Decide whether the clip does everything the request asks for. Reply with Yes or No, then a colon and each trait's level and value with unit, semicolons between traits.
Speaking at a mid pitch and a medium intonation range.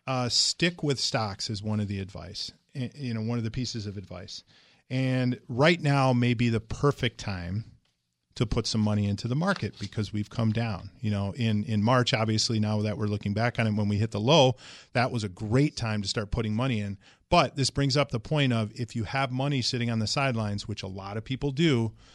No: low, 115 Hz; average, 3.7 semitones